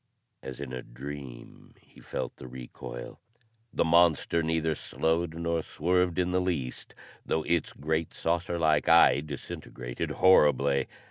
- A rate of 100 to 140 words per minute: Yes, slow, 135 wpm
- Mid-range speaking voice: No, very low, 80 Hz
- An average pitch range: Yes, average, 3.7 semitones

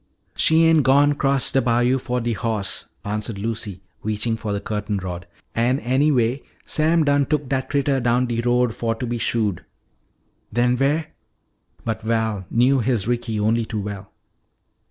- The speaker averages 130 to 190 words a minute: Yes, average, 165 wpm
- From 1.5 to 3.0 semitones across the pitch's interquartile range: No, average, 3.5 semitones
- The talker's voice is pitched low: Yes, low, 120 Hz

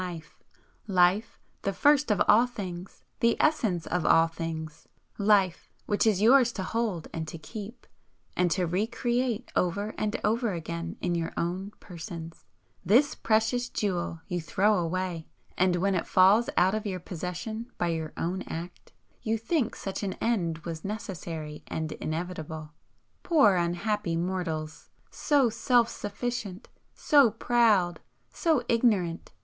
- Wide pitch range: No, average, 4.8 semitones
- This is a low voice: No, high, 190 Hz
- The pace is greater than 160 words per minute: No, average, 140 wpm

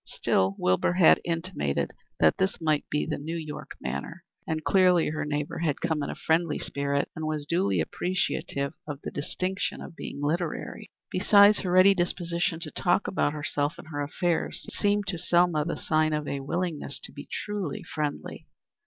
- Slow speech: No, average, 175 wpm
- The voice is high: No, medium, 160 Hz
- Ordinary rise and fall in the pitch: Yes, average, 3.4 semitones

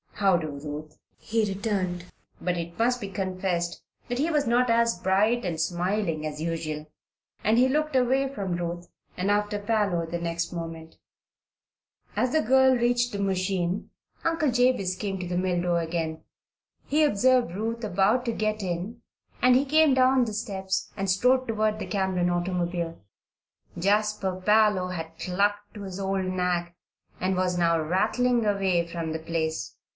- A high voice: Yes, high, 195 Hz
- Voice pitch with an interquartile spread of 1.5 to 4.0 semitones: No, average, 4.8 semitones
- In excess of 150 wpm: Yes, average, 160 wpm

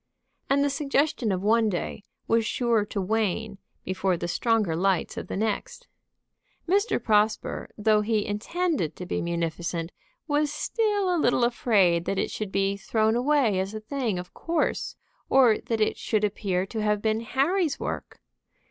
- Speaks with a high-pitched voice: Yes, high, 215 Hz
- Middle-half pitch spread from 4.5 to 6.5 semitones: Yes, average, 5.1 semitones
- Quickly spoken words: No, average, 165 wpm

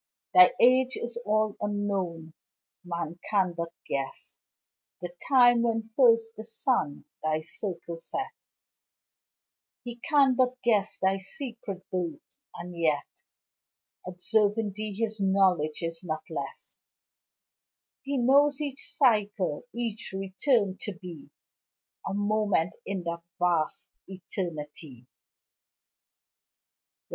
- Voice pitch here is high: Yes, high, 200 Hz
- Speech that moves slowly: Yes, slow, 105 wpm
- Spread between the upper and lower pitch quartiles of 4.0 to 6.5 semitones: Yes, average, 5.2 semitones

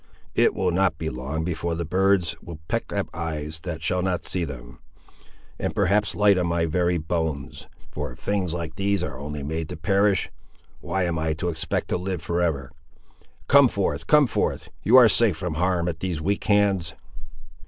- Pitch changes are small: No, average, 3.4 semitones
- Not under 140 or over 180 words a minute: No, average, 190 wpm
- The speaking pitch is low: Yes, very low, 85 Hz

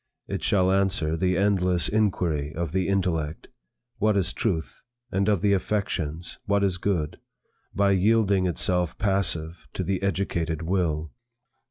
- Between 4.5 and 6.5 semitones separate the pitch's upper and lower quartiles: No, average, 3.2 semitones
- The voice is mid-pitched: No, very low, 95 Hz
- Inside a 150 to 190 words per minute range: No, average, 140 wpm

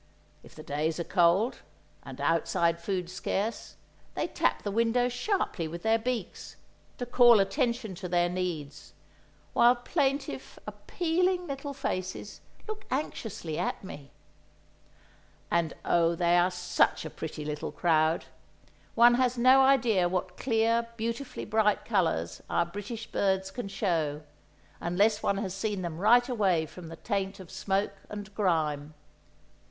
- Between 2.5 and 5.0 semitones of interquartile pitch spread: No, wide, 5.5 semitones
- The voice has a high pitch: Yes, high, 195 Hz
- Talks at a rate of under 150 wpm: Yes, average, 140 wpm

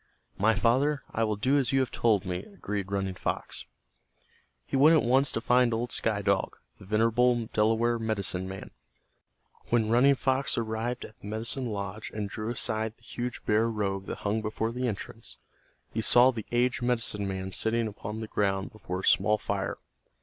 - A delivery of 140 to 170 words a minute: No, average, 180 wpm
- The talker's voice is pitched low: Yes, low, 110 Hz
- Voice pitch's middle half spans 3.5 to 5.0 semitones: No, average, 2.9 semitones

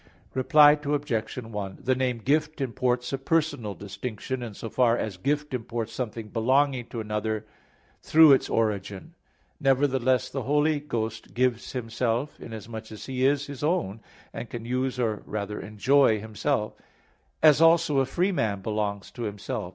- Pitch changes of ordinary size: Yes, average, 4.4 semitones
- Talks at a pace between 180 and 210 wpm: No, average, 150 wpm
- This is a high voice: No, low, 125 Hz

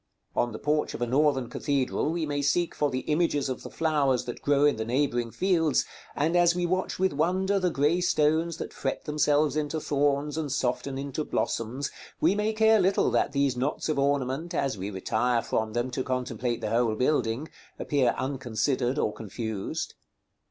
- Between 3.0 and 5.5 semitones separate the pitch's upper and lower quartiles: Yes, average, 4.0 semitones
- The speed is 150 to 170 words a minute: No, average, 185 wpm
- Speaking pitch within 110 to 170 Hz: Yes, medium, 140 Hz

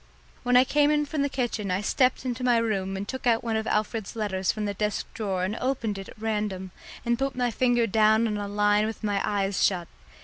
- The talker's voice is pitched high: Yes, high, 215 Hz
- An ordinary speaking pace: No, fast, 230 wpm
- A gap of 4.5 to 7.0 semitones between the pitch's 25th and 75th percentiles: No, average, 3.2 semitones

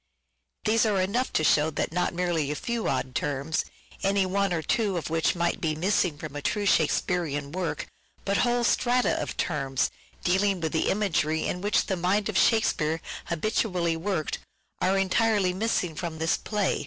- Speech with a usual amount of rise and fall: Yes, average, 4.2 semitones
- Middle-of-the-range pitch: Yes, medium, 180 Hz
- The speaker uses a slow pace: No, average, 175 wpm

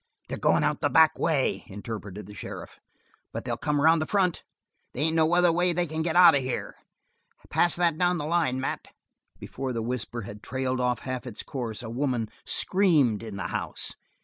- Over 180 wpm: Yes, average, 200 wpm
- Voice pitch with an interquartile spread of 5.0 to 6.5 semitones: Yes, wide, 5.6 semitones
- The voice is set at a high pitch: No, medium, 140 Hz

